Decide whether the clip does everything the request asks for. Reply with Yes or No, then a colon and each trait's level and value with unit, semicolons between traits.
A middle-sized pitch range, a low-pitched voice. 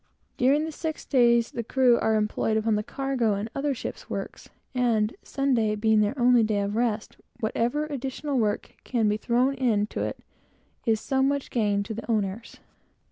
No: average, 3.7 semitones; high, 235 Hz